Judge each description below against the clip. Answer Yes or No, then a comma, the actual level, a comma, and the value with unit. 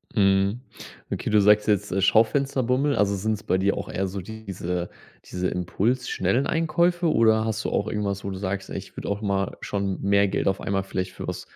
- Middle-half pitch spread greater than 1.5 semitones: Yes, narrow, 2.4 semitones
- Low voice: Yes, low, 100 Hz